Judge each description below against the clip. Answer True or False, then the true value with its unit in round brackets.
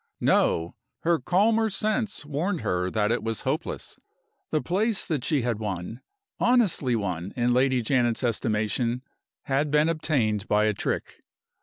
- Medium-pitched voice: False (125 Hz)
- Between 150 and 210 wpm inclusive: False (140 wpm)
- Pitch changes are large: True (7.4 semitones)